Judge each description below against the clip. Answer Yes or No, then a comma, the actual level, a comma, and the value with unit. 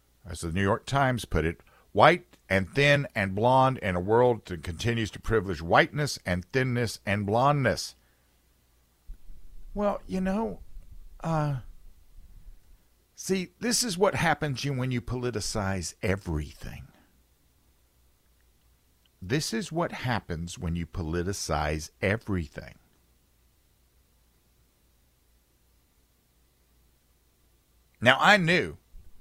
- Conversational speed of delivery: No, slow, 100 wpm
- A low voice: Yes, very low, 90 Hz